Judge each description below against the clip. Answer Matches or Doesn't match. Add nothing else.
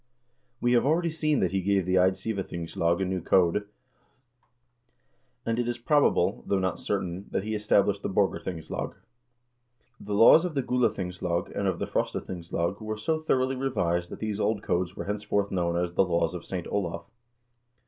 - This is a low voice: Matches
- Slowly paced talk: Doesn't match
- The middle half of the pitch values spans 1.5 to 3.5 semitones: Doesn't match